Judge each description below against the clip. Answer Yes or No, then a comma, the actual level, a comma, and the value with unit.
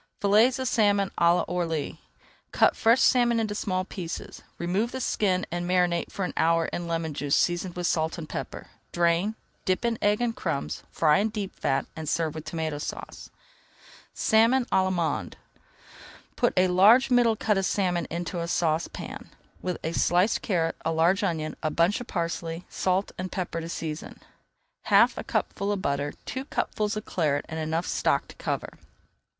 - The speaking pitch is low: No, medium, 180 Hz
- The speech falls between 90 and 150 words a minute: No, average, 175 wpm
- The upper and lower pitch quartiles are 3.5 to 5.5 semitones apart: Yes, average, 3.9 semitones